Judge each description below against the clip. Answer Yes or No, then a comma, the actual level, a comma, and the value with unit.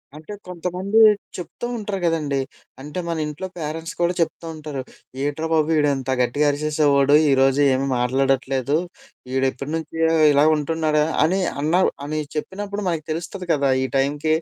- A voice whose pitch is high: No, medium, 150 Hz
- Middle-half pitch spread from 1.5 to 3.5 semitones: Yes, average, 3.0 semitones